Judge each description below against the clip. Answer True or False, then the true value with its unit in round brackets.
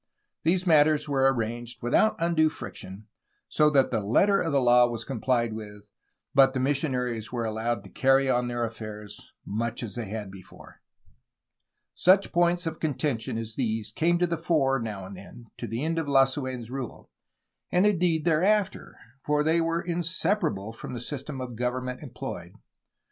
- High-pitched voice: False (130 Hz)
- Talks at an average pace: True (165 wpm)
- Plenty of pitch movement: True (5.7 semitones)